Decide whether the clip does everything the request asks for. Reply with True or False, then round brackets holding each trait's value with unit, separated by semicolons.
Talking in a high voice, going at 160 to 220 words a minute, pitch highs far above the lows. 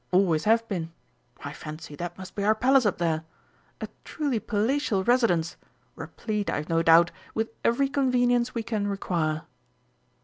False (205 Hz; 150 wpm; 6.1 semitones)